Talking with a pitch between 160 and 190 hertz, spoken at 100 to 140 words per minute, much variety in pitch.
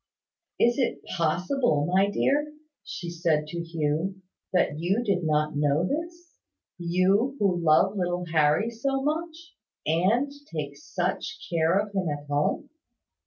Yes: medium, 185 Hz; slow, 135 wpm; wide, 7.1 semitones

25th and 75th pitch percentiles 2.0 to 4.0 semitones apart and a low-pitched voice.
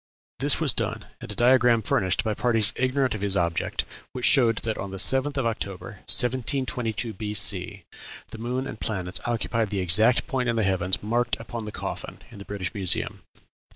Yes: average, 3.7 semitones; low, 110 Hz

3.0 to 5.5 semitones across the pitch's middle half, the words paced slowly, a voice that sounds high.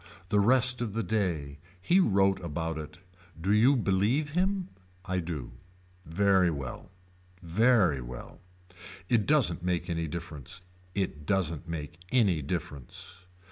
No: average, 5.2 semitones; slow, 130 wpm; very low, 90 Hz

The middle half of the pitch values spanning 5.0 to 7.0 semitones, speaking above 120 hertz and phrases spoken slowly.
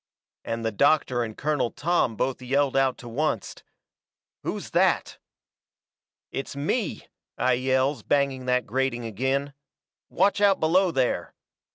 No: average, 2.7 semitones; low, 135 Hz; slow, 130 wpm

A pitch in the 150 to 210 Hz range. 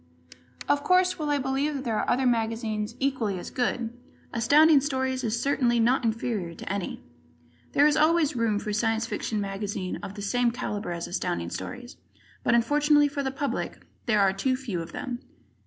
No: high, 240 Hz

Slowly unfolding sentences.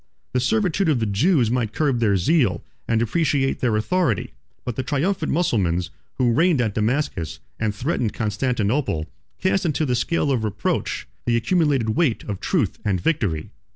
No: average, 160 wpm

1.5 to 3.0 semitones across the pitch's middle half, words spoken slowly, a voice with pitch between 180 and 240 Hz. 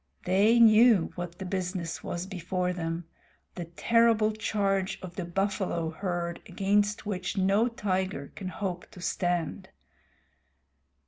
Yes: average, 2.7 semitones; slow, 125 wpm; medium, 185 Hz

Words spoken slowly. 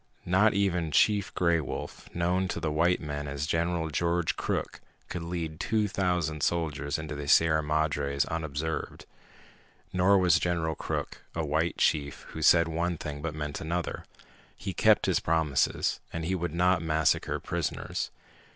No: average, 155 wpm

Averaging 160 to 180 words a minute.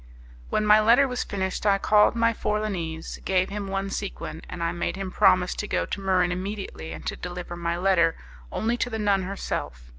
No: fast, 205 wpm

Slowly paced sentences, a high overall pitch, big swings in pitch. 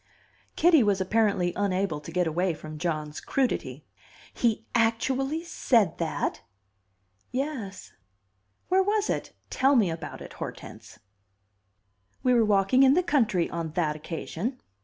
Yes: slow, 130 wpm; high, 205 Hz; wide, 7.4 semitones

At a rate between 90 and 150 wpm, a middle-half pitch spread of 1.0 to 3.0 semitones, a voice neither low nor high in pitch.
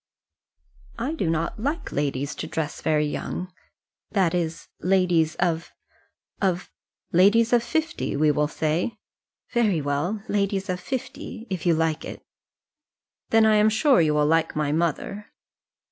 No: average, 145 wpm; average, 5.3 semitones; medium, 180 Hz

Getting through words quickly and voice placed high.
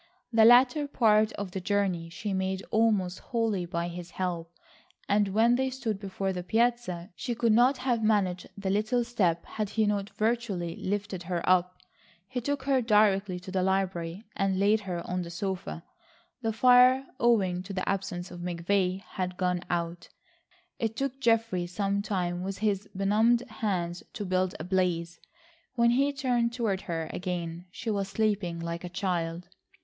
No: average, 170 wpm; high, 195 Hz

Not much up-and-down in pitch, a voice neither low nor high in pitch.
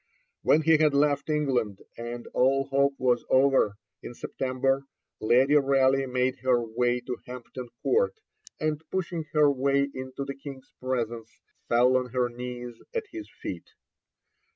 No: narrow, 2.3 semitones; low, 130 Hz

